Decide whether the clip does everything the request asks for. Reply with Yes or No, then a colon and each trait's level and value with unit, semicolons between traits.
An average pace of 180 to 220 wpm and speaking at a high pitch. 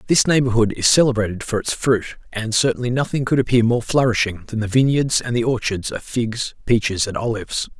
No: average, 190 wpm; low, 120 Hz